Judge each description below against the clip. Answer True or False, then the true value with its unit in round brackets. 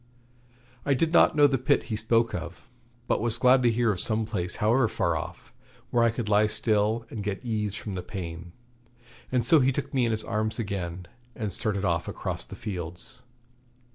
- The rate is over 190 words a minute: True (200 wpm)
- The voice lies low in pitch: True (110 Hz)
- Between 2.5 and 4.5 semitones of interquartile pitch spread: True (3.5 semitones)